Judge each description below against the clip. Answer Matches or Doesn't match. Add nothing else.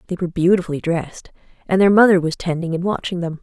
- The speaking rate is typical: Doesn't match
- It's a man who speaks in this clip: Doesn't match